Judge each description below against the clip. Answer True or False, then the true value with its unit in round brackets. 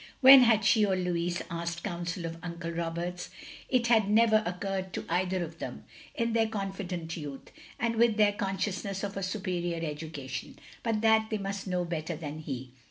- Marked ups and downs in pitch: False (3.9 semitones)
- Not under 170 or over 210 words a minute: True (175 wpm)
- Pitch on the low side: False (185 Hz)